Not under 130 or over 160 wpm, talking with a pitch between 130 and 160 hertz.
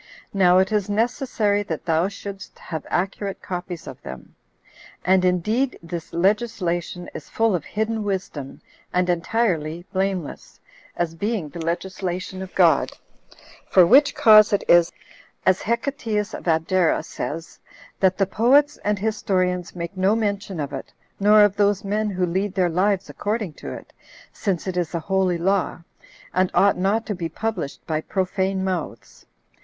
No: average, 155 wpm; high, 190 Hz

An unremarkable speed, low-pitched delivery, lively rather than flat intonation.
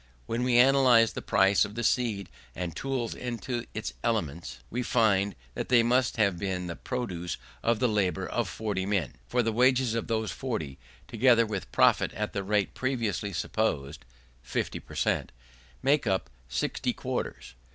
No: average, 165 wpm; low, 110 Hz; average, 4.2 semitones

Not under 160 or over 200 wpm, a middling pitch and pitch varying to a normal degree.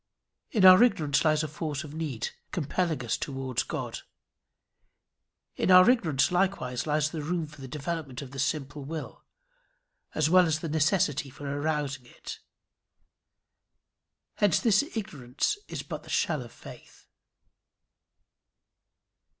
No: slow, 135 wpm; medium, 155 Hz; average, 3.6 semitones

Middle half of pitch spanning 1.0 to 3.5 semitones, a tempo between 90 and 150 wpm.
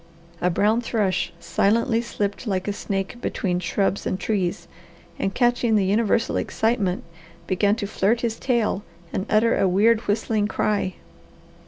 Yes: average, 2.9 semitones; average, 145 wpm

